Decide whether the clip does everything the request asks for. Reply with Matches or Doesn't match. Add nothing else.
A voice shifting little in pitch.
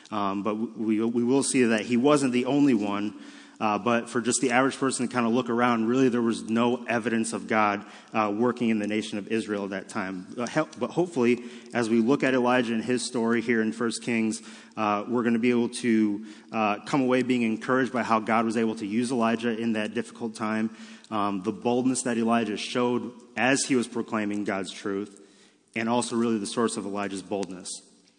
Matches